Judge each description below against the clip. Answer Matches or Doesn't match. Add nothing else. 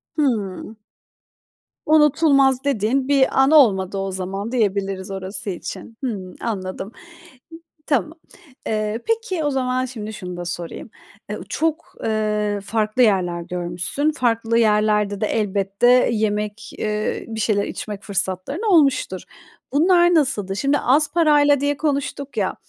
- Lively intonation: Matches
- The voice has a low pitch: Doesn't match